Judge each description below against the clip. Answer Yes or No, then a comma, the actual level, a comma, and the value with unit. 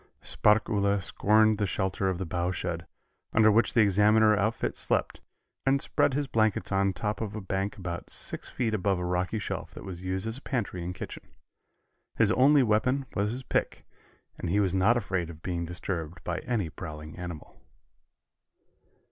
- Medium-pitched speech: No, low, 100 Hz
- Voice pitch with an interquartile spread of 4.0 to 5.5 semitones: No, average, 3.5 semitones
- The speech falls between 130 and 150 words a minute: No, average, 175 wpm